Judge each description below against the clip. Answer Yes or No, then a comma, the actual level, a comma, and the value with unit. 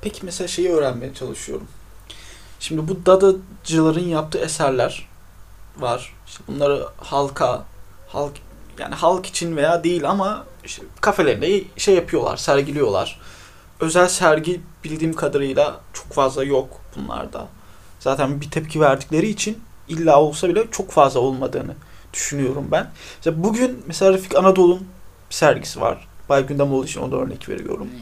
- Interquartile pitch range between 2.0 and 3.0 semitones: No, wide, 5.4 semitones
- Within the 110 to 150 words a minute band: Yes, average, 135 wpm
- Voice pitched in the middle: Yes, medium, 155 Hz